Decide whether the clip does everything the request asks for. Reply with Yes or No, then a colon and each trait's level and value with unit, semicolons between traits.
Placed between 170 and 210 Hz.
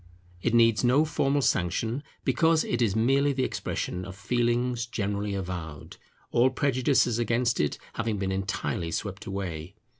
No: low, 115 Hz